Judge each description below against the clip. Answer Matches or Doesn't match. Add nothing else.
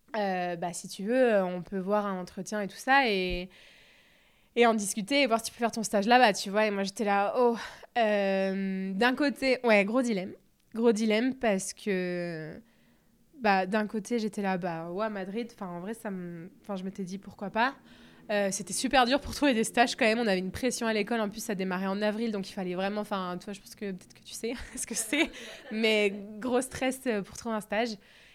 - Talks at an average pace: Doesn't match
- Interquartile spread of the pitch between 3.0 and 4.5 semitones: Matches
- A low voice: Doesn't match